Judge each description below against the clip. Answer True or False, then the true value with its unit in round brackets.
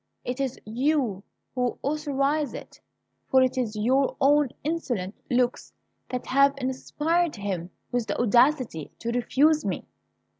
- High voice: True (255 Hz)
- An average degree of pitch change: True (3.5 semitones)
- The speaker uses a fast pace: False (135 wpm)